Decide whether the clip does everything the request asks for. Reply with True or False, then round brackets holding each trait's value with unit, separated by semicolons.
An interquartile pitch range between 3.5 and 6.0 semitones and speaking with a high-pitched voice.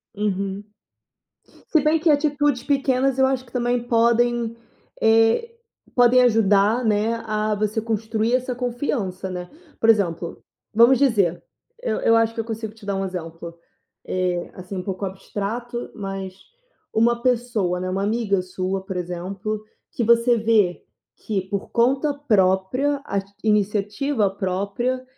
True (3.9 semitones; 220 Hz)